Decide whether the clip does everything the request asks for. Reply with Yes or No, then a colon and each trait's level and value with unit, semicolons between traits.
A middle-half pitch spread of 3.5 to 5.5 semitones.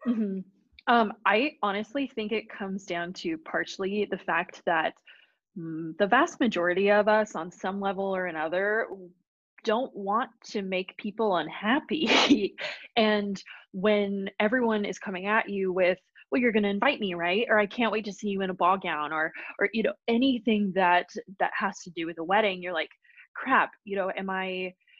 No: average, 3.1 semitones